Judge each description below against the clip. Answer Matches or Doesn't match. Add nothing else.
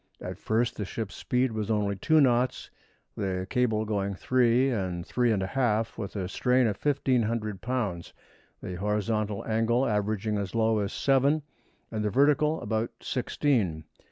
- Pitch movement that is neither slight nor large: Matches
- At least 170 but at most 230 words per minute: Doesn't match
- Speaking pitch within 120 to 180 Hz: Doesn't match